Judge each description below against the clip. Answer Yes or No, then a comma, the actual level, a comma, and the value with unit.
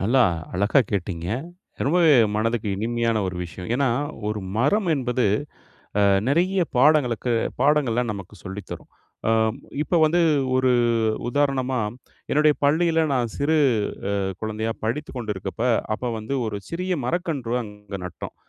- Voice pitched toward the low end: Yes, low, 125 Hz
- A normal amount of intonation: No, wide, 5.7 semitones